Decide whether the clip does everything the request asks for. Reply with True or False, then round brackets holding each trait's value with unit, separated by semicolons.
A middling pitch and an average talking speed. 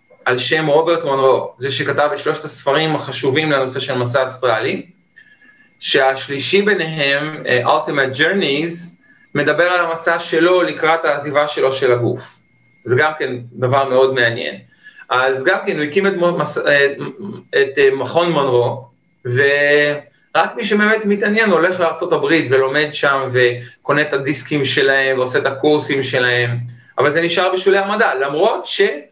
True (145 Hz; 135 wpm)